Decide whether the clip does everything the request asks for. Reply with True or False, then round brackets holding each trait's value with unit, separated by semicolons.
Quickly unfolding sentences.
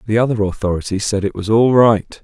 True (215 wpm)